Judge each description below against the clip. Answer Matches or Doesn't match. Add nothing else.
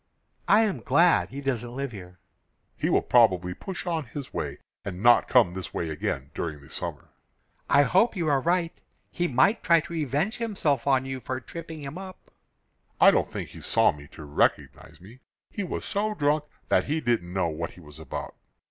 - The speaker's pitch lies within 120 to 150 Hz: Matches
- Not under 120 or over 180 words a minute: Doesn't match